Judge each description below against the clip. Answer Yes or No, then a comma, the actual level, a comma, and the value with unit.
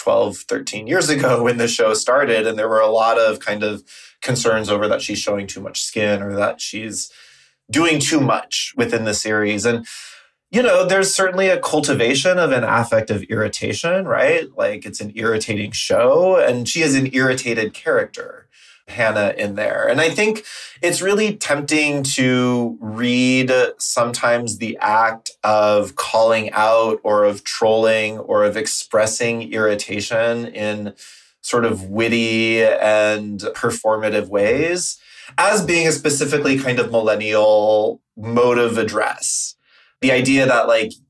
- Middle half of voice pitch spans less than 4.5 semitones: Yes, average, 4.1 semitones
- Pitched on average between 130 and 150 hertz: No, low, 115 Hz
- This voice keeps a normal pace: Yes, average, 150 wpm